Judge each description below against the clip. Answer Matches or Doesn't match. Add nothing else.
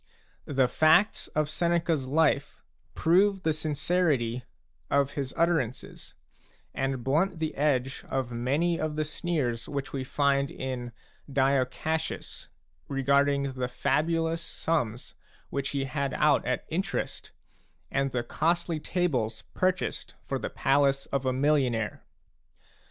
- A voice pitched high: Doesn't match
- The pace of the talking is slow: Matches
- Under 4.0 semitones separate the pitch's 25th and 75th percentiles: Matches